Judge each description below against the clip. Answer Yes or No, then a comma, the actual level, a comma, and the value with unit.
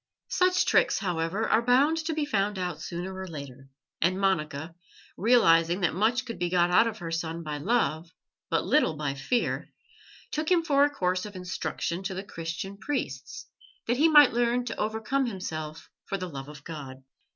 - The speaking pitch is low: No, medium, 185 Hz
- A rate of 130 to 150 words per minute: No, average, 185 wpm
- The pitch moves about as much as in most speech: No, wide, 6.6 semitones